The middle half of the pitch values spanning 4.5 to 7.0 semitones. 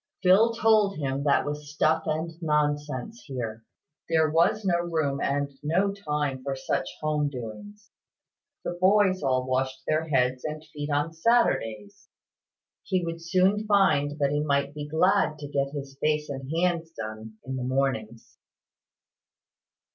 No: average, 3.9 semitones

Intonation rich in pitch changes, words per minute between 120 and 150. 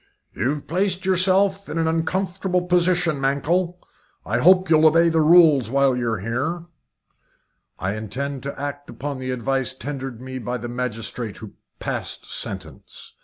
Yes: wide, 5.7 semitones; average, 145 wpm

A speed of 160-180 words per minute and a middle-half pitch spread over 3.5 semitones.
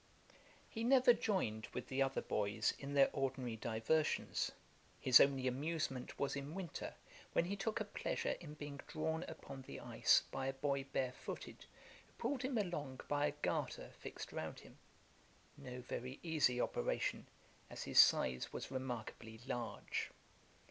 No: average, 150 wpm; average, 4.1 semitones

